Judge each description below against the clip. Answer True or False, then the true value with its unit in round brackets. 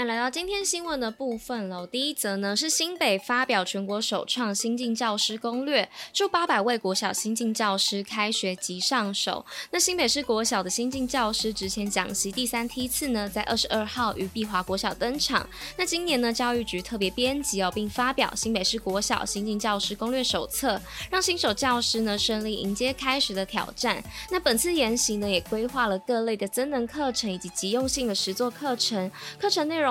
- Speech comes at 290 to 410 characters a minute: True (300 characters per minute)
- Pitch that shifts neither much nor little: True (4.2 semitones)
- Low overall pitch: False (230 Hz)